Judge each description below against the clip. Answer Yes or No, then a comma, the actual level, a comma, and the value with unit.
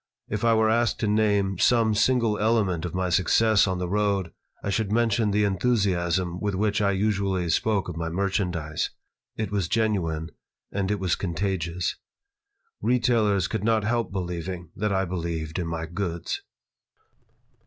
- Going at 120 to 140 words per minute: No, average, 155 wpm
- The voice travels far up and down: No, average, 3.4 semitones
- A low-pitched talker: Yes, low, 100 Hz